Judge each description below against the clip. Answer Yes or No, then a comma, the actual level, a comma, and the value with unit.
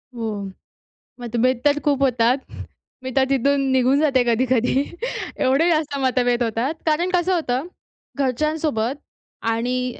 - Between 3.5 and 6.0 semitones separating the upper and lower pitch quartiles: No, average, 3.0 semitones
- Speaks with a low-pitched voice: No, very high, 260 Hz